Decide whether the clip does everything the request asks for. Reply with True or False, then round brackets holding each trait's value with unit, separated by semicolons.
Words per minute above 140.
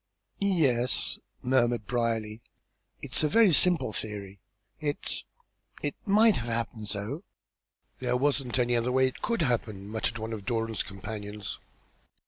False (135 wpm)